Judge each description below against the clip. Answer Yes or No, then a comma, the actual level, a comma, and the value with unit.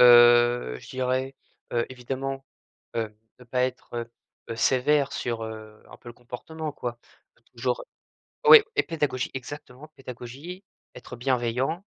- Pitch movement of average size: No, narrow, 2.2 semitones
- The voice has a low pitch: Yes, low, 125 Hz